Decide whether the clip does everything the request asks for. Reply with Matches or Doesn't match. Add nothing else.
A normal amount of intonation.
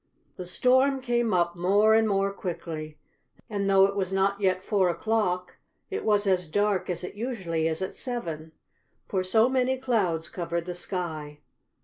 Matches